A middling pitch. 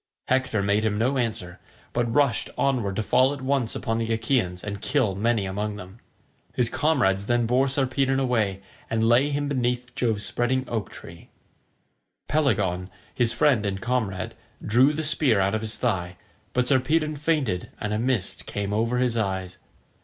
No: low, 115 Hz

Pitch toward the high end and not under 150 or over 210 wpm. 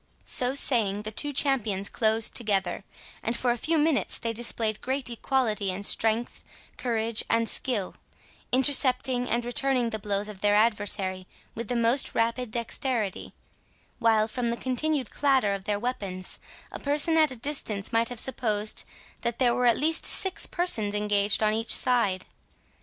Yes: high, 230 Hz; average, 160 wpm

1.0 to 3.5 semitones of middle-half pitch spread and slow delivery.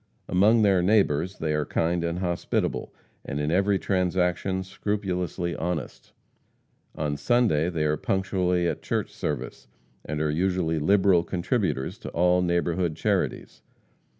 Yes: average, 2.9 semitones; slow, 130 wpm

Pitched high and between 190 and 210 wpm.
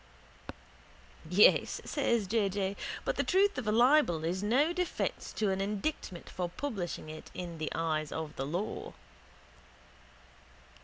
No: high, 195 Hz; average, 140 wpm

